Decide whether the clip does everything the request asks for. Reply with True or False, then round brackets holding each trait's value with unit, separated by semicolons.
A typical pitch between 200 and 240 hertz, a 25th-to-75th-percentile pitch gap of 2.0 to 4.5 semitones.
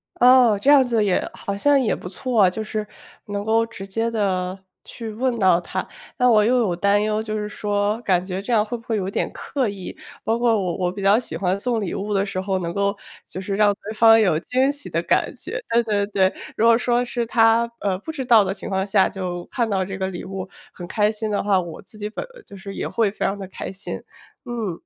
True (210 Hz; 3.0 semitones)